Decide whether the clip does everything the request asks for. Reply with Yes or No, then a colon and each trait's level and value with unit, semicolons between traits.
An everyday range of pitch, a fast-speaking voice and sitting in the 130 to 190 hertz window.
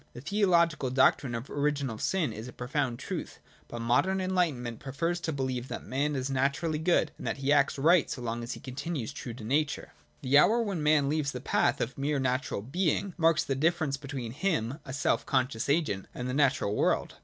Yes: average, 4.0 semitones; fast, 210 wpm; medium, 140 Hz